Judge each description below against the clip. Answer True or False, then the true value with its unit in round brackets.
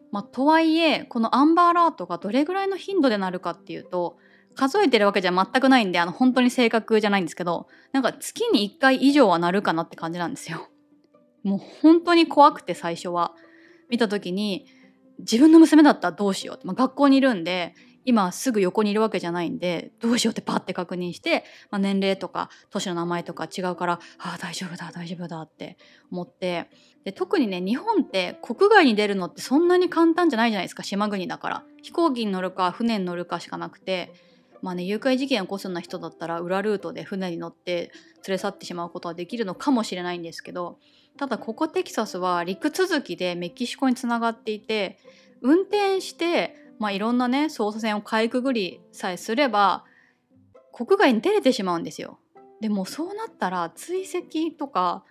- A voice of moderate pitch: False (215 Hz)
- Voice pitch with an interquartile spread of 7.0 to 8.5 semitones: True (7.9 semitones)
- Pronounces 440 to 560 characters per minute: False (395 characters per minute)